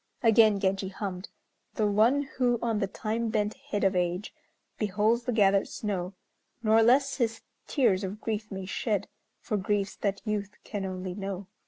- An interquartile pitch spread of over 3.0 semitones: No, narrow, 2.5 semitones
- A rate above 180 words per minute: No, average, 165 wpm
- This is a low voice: No, high, 210 Hz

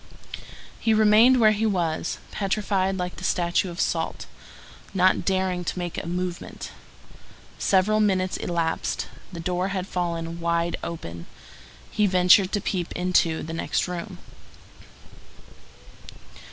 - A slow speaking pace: Yes, slow, 125 wpm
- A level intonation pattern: Yes, narrow, 2.3 semitones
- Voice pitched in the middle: Yes, medium, 180 Hz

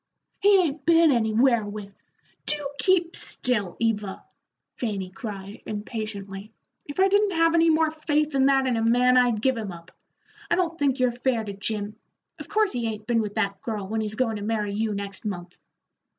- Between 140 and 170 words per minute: No, average, 195 wpm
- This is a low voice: No, high, 230 Hz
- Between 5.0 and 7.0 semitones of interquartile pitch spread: Yes, wide, 5.6 semitones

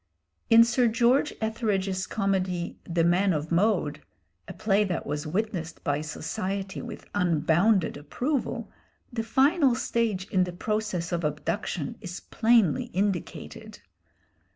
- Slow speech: Yes, slow, 125 wpm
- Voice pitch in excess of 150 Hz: Yes, high, 190 Hz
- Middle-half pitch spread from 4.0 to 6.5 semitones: Yes, average, 4.6 semitones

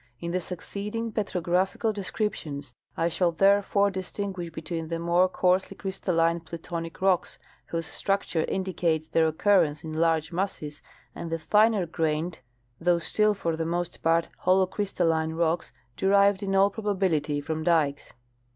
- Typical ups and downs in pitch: Yes, average, 3.1 semitones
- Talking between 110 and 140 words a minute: Yes, slow, 135 wpm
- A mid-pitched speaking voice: Yes, medium, 175 Hz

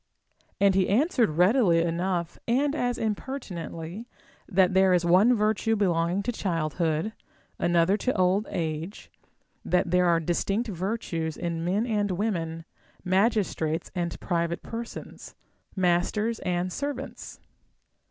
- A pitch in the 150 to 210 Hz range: Yes, medium, 185 Hz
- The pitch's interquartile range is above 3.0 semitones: Yes, average, 4.3 semitones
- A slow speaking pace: Yes, slow, 120 wpm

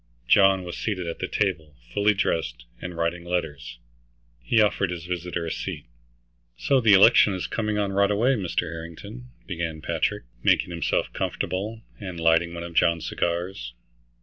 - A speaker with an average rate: Yes, average, 160 wpm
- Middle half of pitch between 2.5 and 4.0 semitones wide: Yes, average, 3.4 semitones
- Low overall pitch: Yes, very low, 90 Hz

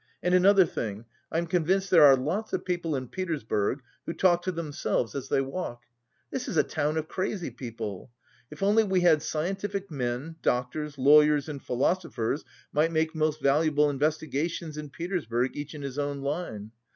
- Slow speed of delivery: No, average, 170 wpm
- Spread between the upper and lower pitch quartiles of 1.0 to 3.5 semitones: No, average, 4.3 semitones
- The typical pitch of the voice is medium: Yes, medium, 150 Hz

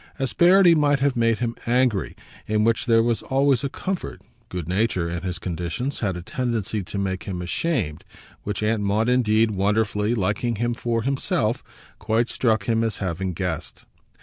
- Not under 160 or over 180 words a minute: Yes, average, 170 wpm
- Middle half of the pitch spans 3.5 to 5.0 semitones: Yes, average, 4.2 semitones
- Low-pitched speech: Yes, low, 110 Hz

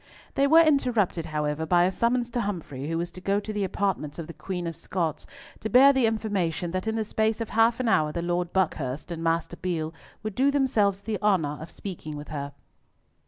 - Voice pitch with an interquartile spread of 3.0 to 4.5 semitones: No, average, 5.2 semitones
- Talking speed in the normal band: No, fast, 215 wpm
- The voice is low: No, medium, 185 Hz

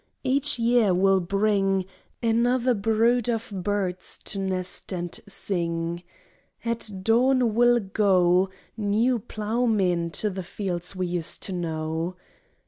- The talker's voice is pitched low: No, high, 200 Hz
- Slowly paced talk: Yes, slow, 120 wpm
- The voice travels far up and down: No, average, 4.2 semitones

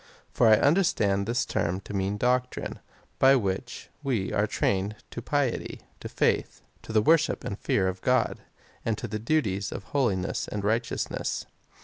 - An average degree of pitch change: Yes, average, 4.3 semitones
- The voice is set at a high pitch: No, low, 110 Hz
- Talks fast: No, average, 155 wpm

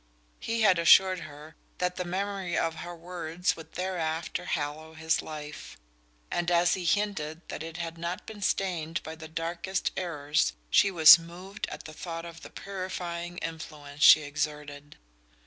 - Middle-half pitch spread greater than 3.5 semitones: No, narrow, 2.5 semitones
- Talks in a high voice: No, medium, 170 Hz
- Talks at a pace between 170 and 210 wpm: No, average, 155 wpm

